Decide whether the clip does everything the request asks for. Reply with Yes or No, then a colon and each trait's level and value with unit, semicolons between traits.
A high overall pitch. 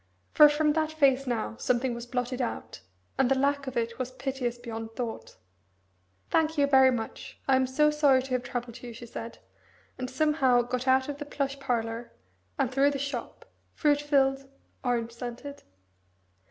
Yes: very high, 260 Hz